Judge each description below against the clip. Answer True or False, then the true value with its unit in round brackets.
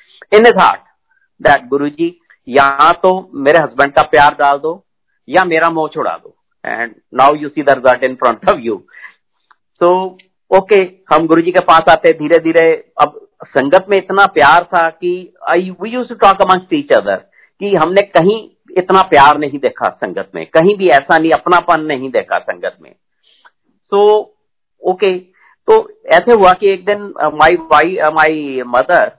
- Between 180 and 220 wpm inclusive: False (170 wpm)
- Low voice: False (175 Hz)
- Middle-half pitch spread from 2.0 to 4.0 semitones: False (4.4 semitones)